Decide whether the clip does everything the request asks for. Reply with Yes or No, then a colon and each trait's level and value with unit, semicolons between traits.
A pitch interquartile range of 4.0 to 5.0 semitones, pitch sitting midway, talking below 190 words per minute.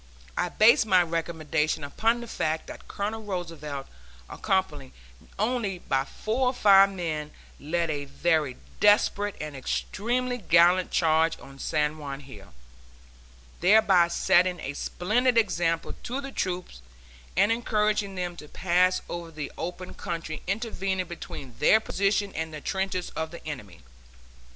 Yes: average, 4.7 semitones; medium, 175 Hz; slow, 135 wpm